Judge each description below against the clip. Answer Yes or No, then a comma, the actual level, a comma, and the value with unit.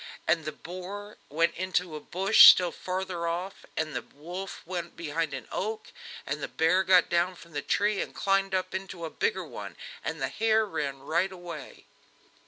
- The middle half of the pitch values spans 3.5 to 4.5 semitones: No, narrow, 2.6 semitones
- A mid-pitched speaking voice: Yes, medium, 180 Hz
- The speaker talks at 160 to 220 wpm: Yes, average, 185 wpm